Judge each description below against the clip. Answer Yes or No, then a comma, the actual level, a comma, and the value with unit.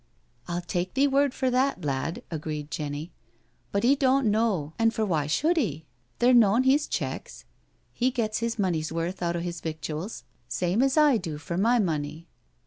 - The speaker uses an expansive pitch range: Yes, wide, 7.6 semitones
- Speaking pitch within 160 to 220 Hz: Yes, high, 190 Hz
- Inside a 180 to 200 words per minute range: Yes, average, 185 wpm